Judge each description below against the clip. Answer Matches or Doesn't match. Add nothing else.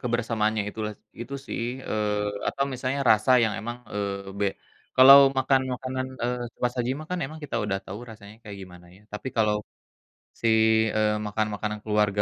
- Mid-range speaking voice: Doesn't match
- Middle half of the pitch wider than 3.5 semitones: Doesn't match